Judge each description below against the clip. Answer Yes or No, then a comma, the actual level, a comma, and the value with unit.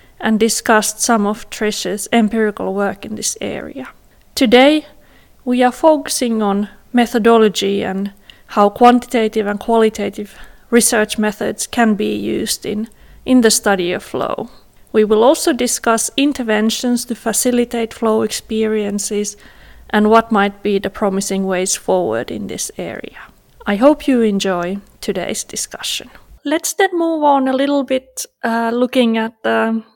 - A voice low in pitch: No, high, 225 Hz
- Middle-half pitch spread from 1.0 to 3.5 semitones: Yes, average, 3.1 semitones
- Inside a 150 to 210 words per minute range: No, average, 140 wpm